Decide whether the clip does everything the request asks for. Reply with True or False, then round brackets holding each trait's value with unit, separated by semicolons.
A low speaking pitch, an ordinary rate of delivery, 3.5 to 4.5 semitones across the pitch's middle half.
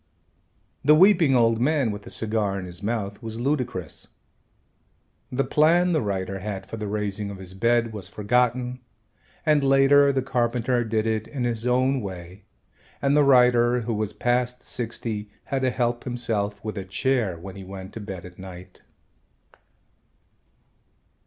True (115 Hz; 160 wpm; 4.0 semitones)